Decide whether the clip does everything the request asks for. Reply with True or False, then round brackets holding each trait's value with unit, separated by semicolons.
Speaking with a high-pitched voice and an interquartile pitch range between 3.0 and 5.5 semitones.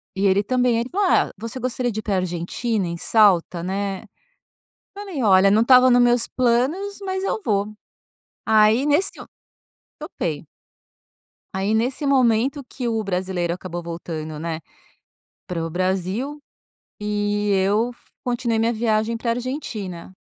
True (220 Hz; 4.7 semitones)